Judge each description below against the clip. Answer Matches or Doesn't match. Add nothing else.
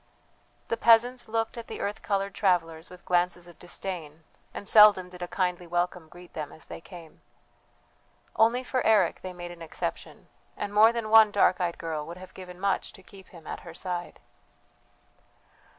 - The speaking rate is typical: Matches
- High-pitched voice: Doesn't match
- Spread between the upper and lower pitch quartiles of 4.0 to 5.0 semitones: Doesn't match